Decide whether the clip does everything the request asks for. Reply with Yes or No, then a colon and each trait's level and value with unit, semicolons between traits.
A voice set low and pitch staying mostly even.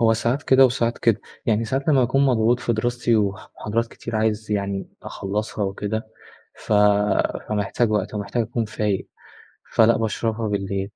Yes: low, 110 Hz; narrow, 2.2 semitones